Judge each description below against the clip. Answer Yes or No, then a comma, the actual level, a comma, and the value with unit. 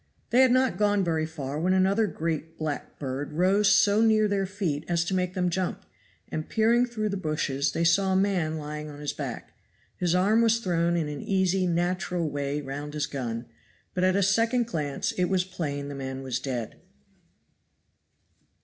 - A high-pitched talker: No, medium, 175 Hz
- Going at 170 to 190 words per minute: Yes, average, 185 wpm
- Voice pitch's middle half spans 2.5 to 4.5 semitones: No, average, 4.9 semitones